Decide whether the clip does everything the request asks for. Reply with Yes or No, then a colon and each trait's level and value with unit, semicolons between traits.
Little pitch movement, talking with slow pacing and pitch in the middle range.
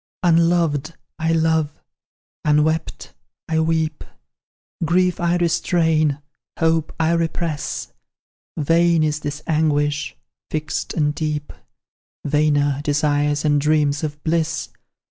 Yes: narrow, 1.8 semitones; slow, 100 wpm; medium, 155 Hz